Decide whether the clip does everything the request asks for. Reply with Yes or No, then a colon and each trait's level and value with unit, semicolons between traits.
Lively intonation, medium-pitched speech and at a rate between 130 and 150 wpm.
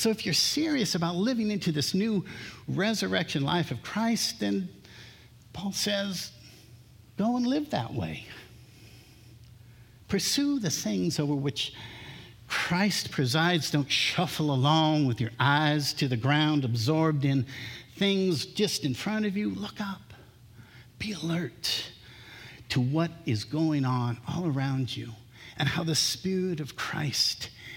Yes: wide, 6.9 semitones; medium, 145 Hz; slow, 135 wpm